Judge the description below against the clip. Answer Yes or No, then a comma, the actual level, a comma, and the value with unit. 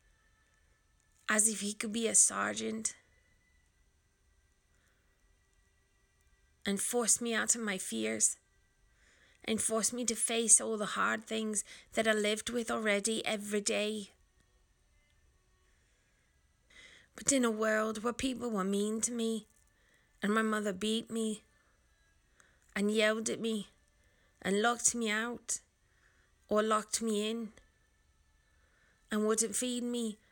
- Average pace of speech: No, slow, 120 wpm